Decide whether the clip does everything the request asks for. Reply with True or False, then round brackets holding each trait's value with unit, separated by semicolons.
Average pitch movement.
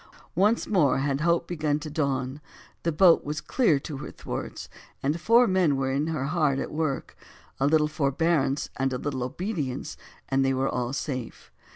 True (3.5 semitones)